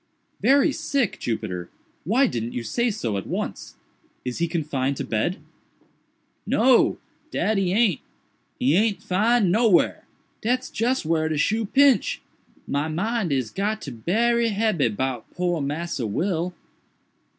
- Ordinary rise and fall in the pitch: No, wide, 8.3 semitones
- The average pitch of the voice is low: No, medium, 180 Hz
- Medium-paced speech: No, slow, 130 wpm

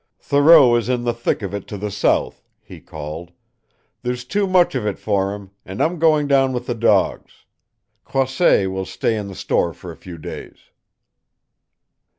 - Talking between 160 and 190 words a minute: Yes, average, 175 wpm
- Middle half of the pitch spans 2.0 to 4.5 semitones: No, wide, 5.6 semitones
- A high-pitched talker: No, low, 115 Hz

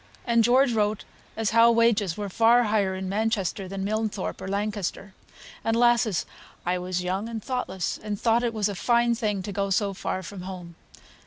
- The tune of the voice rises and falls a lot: No, average, 3.1 semitones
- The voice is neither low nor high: No, high, 210 Hz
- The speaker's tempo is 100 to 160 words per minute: No, average, 185 wpm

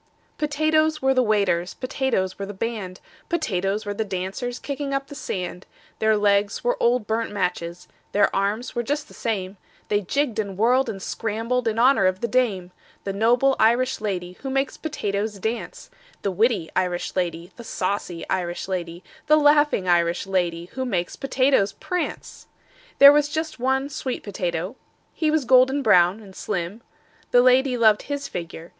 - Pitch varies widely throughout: Yes, wide, 5.9 semitones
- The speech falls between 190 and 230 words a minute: No, average, 165 wpm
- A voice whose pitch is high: Yes, high, 220 Hz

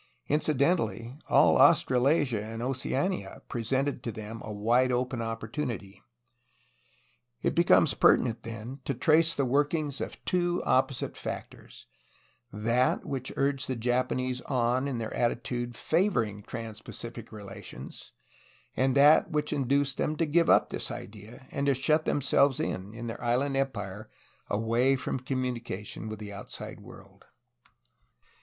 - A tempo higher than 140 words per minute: No, slow, 135 wpm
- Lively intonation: No, average, 3.7 semitones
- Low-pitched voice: Yes, low, 125 Hz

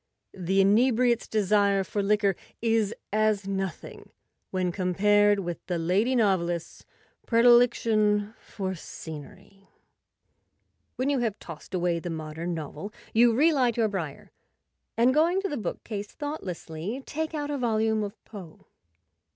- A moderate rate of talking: No, slow, 130 wpm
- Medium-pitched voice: No, high, 205 Hz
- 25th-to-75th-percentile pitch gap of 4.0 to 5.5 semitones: Yes, average, 4.4 semitones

